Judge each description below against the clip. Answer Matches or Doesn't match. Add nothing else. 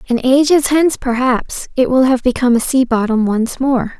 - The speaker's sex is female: Matches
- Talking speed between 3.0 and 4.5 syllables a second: Doesn't match